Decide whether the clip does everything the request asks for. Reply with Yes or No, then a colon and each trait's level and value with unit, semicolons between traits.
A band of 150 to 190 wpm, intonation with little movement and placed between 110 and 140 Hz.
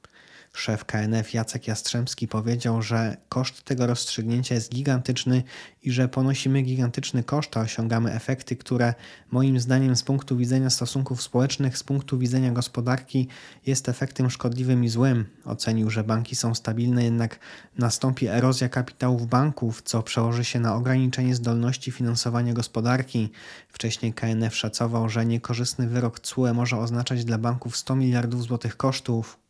No: average, 140 wpm; narrow, 1.8 semitones; low, 120 Hz